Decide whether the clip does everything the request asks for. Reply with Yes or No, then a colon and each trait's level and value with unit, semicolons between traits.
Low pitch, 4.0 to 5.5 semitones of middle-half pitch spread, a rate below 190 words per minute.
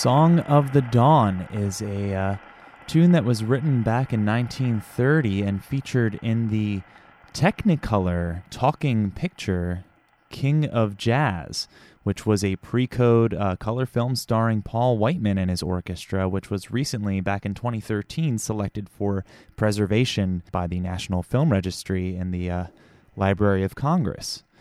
Yes: low, 105 Hz; average, 4.3 semitones; average, 140 wpm